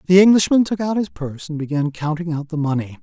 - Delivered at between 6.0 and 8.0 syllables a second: Yes, 6.4 syllables/s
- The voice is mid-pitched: Yes, medium, 165 Hz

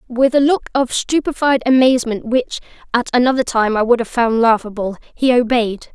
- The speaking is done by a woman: Yes, female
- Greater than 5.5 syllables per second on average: No, 5.3 syllables/s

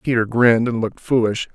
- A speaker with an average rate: Yes, average, 195 wpm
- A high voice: No, low, 115 Hz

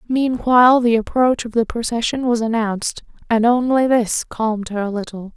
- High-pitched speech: Yes, high, 230 Hz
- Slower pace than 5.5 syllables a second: Yes, 5.1 syllables/s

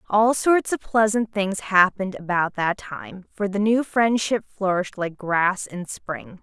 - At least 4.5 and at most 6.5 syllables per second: No, 4.1 syllables/s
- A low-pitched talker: No, high, 200 Hz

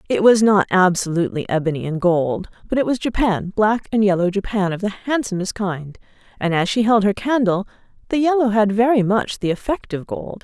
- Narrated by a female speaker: Yes, female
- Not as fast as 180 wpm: No, average, 195 wpm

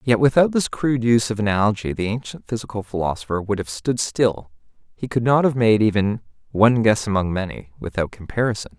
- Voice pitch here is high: No, low, 110 Hz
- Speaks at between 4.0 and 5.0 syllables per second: No, 6.0 syllables/s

